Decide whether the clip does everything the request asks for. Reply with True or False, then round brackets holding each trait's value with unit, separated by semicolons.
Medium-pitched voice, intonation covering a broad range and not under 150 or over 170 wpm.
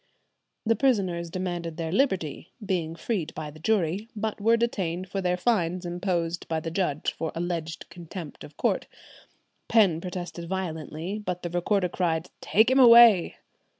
False (180 Hz; 3.4 semitones; 155 wpm)